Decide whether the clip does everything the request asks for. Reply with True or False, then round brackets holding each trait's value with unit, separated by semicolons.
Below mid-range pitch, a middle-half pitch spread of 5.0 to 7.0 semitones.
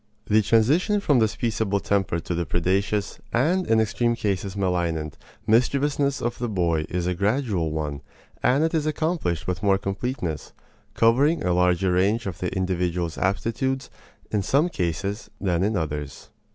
True (100 Hz; 5.3 semitones)